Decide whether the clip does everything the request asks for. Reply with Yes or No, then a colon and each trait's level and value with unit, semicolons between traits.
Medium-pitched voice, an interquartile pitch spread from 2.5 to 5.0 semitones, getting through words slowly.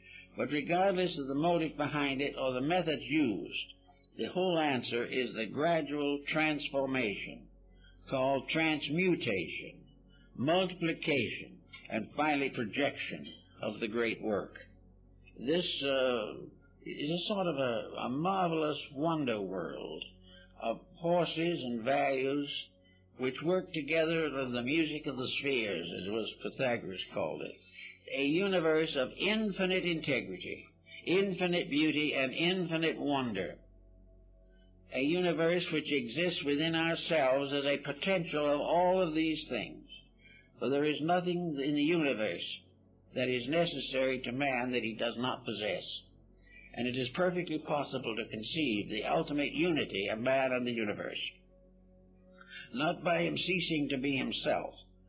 No: medium, 145 Hz; wide, 5.5 semitones; slow, 130 wpm